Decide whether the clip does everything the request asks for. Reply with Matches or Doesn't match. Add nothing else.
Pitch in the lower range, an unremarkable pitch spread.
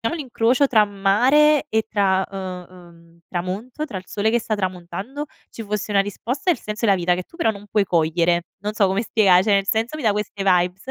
Doesn't match